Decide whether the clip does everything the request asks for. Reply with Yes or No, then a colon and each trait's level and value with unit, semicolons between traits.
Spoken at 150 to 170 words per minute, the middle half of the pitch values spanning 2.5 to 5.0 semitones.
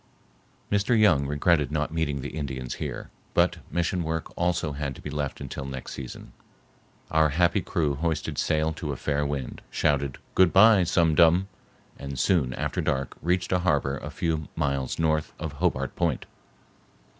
Yes: average, 165 wpm; average, 3.4 semitones